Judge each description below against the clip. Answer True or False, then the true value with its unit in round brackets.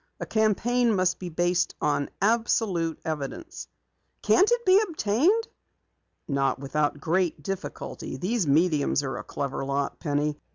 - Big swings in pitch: True (7.7 semitones)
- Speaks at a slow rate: True (130 wpm)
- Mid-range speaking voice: True (175 Hz)